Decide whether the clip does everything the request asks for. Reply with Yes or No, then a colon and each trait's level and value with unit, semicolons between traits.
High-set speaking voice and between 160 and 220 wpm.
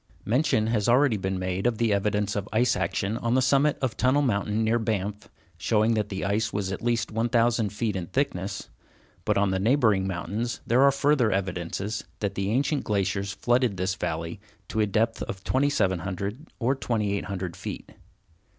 No: low, 105 Hz; average, 175 wpm